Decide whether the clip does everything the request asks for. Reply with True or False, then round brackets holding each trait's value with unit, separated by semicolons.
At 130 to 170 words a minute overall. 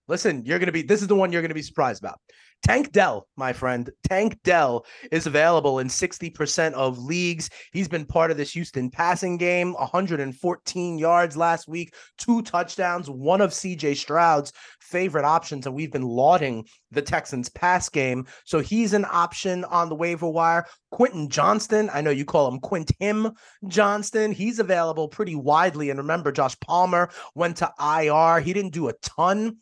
False (180 wpm)